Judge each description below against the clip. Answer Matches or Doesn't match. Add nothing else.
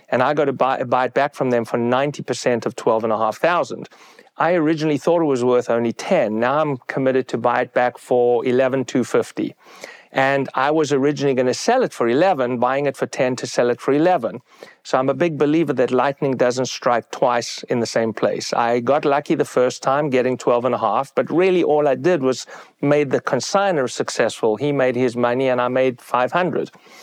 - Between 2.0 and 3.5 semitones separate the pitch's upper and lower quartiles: Matches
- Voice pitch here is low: Matches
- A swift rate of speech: Matches